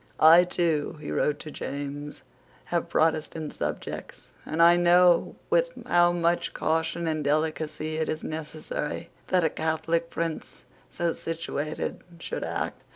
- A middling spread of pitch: No, narrow, 1.6 semitones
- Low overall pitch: No, medium, 160 Hz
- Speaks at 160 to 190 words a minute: No, slow, 135 wpm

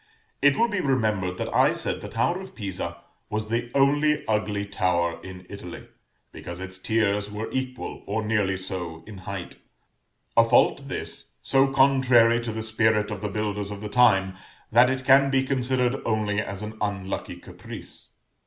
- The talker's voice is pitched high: No, low, 110 Hz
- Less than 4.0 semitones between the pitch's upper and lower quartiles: No, average, 4.6 semitones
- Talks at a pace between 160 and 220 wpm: Yes, average, 170 wpm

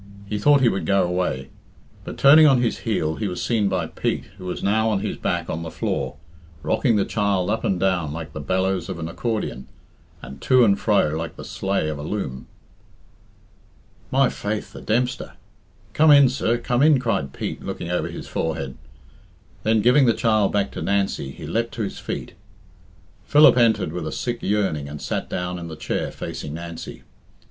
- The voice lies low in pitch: Yes, low, 100 Hz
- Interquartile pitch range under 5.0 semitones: No, wide, 5.6 semitones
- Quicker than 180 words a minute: Yes, average, 190 wpm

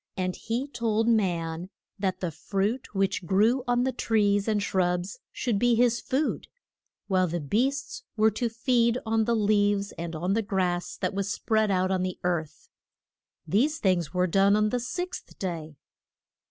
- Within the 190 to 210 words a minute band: No, average, 165 wpm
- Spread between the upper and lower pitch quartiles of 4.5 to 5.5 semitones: No, average, 4.0 semitones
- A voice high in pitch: Yes, high, 205 Hz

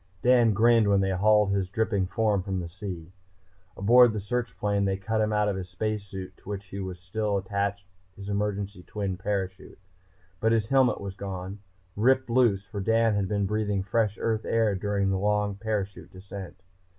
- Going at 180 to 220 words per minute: Yes, average, 185 wpm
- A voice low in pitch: Yes, low, 100 Hz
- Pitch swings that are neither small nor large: No, narrow, 2.1 semitones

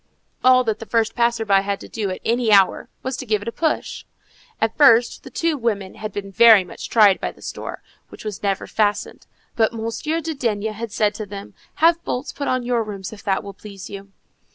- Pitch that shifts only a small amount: No, average, 3.0 semitones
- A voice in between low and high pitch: No, high, 220 Hz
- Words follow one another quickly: Yes, fast, 225 wpm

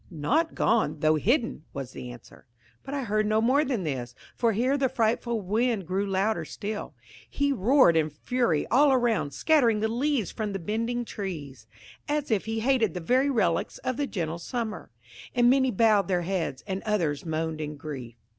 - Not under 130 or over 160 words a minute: No, average, 185 wpm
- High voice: Yes, high, 215 Hz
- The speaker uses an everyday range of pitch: No, wide, 7.0 semitones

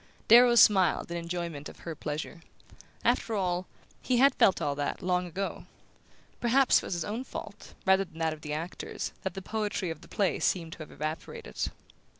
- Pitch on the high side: No, medium, 180 Hz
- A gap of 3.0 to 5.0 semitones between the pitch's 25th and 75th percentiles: Yes, average, 4.0 semitones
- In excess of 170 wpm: Yes, average, 185 wpm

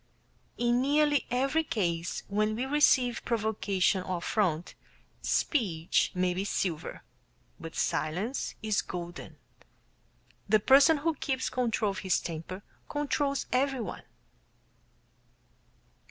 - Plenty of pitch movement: Yes, wide, 6.8 semitones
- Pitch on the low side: No, high, 215 Hz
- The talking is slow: Yes, slow, 105 wpm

